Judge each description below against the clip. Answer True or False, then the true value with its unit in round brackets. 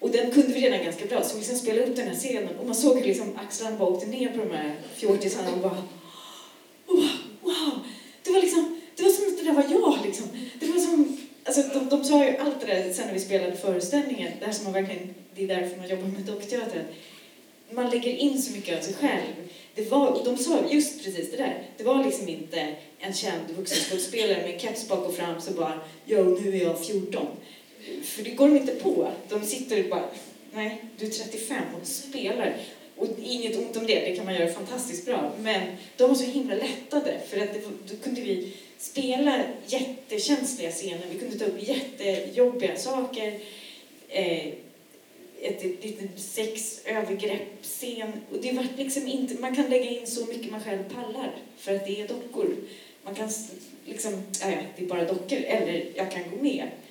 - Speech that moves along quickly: True (200 wpm)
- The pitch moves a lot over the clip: True (5.7 semitones)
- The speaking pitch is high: True (225 Hz)